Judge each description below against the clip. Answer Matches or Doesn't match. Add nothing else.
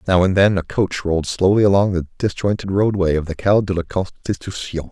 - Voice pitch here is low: Matches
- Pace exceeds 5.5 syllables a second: Matches